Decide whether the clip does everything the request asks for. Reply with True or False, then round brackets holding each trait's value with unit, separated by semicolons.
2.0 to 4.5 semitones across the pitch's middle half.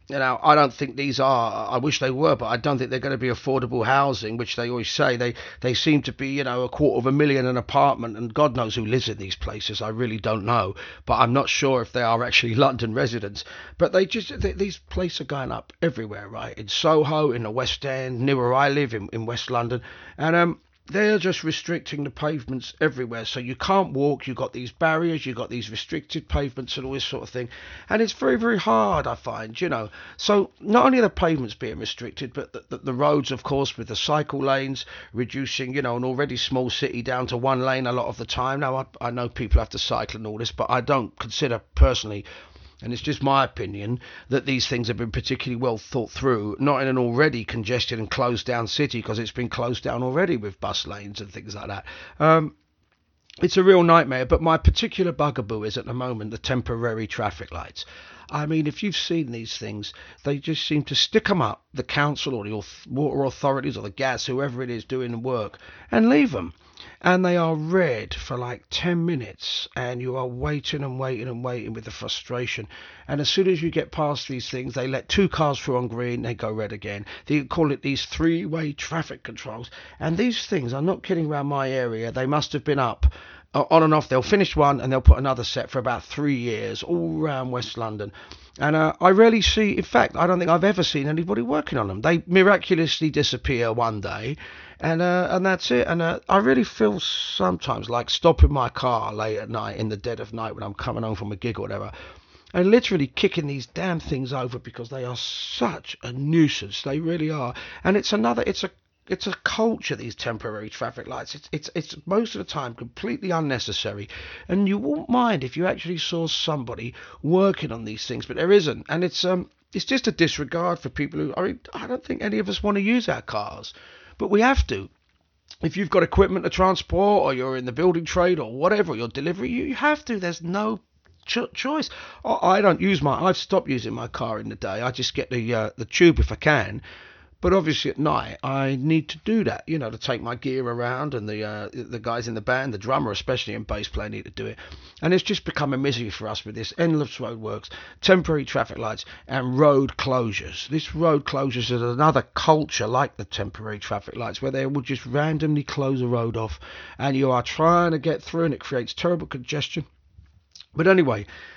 False (5.3 semitones)